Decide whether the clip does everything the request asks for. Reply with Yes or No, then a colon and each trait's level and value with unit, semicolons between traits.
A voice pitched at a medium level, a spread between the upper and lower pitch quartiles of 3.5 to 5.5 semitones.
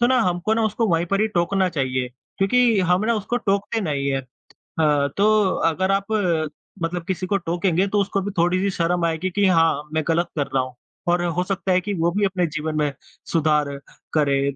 Yes: medium, 175 Hz; average, 3.8 semitones